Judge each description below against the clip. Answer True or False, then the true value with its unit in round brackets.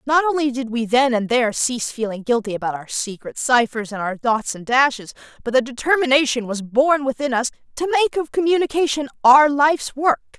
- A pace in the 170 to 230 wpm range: True (190 wpm)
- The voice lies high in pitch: True (260 Hz)